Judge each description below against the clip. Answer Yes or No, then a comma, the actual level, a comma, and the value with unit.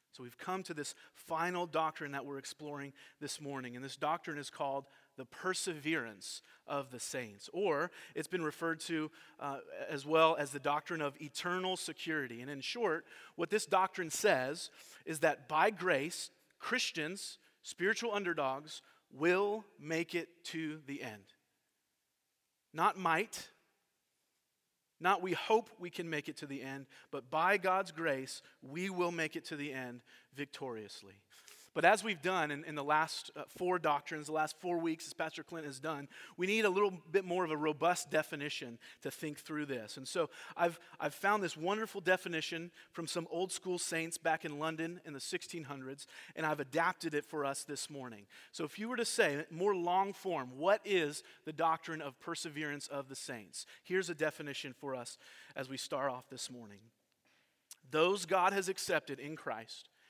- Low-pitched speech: No, medium, 160 Hz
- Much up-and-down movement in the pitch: No, average, 3.8 semitones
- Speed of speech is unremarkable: Yes, average, 175 wpm